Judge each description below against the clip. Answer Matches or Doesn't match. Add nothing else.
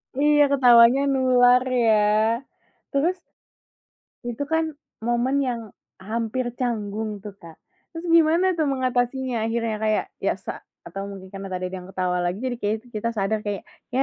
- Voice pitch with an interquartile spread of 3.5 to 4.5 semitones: Matches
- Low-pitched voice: Doesn't match